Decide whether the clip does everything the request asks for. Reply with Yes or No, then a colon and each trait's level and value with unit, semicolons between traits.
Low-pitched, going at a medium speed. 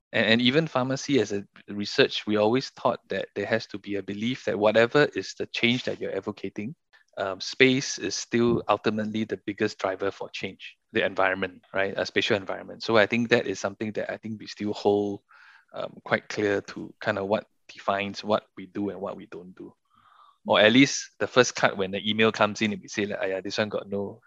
No: low, 110 Hz; fast, 220 wpm